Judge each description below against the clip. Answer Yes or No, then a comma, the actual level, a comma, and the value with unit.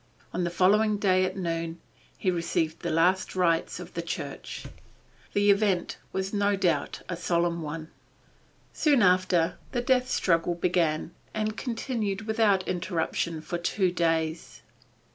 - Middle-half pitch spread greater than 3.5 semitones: No, average, 3.2 semitones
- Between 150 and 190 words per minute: No, average, 140 wpm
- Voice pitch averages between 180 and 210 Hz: Yes, medium, 185 Hz